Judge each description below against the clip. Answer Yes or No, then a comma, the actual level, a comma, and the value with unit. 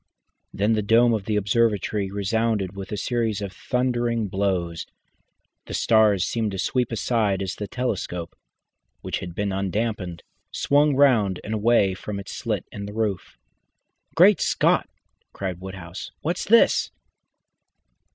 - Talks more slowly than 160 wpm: Yes, average, 140 wpm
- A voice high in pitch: No, low, 105 Hz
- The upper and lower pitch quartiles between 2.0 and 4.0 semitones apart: Yes, average, 3.3 semitones